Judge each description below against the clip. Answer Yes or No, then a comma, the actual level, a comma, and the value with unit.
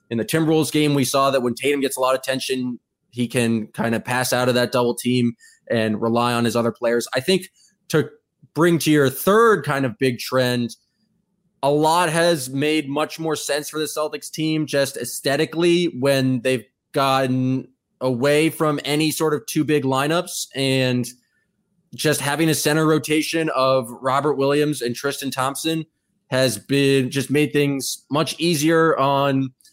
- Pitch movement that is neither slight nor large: Yes, average, 3.3 semitones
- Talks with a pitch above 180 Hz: No, medium, 140 Hz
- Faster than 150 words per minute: Yes, average, 170 wpm